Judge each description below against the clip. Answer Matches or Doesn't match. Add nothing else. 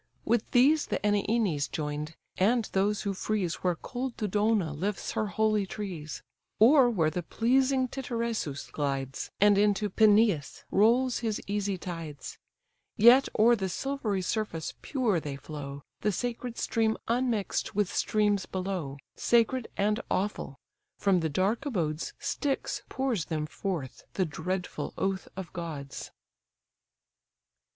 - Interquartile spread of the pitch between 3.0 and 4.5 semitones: Doesn't match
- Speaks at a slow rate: Matches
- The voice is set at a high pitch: Matches